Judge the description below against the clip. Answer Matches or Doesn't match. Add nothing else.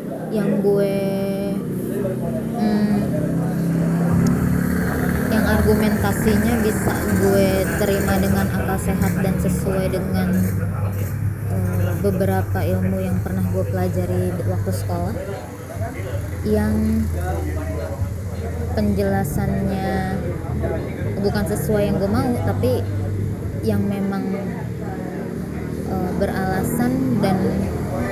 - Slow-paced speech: Matches